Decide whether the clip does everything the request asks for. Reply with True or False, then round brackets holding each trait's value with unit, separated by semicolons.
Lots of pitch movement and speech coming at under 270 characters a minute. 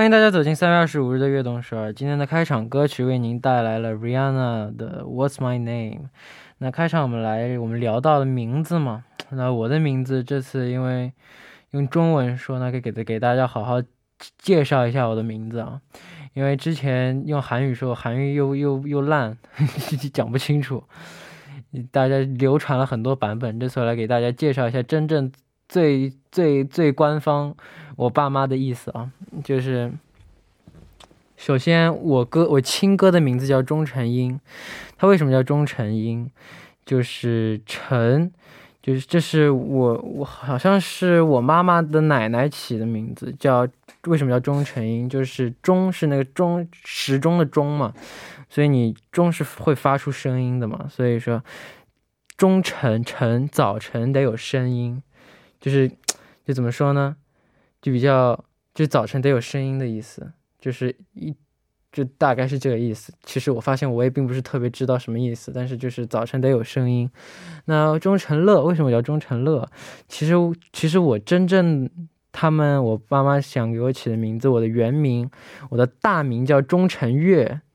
False (3.5 semitones; 260 characters per minute)